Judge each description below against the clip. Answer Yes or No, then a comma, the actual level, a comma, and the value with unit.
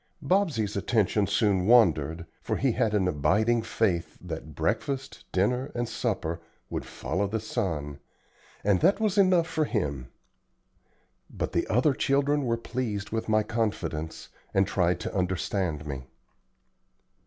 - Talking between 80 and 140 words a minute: Yes, slow, 135 wpm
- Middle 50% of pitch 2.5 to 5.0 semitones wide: No, wide, 5.5 semitones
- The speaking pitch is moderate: No, low, 105 Hz